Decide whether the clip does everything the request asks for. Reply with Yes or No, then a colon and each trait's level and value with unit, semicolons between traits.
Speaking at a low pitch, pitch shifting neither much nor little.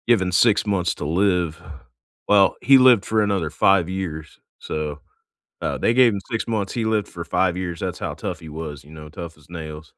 Yes: very low, 90 Hz; average, 4.7 semitones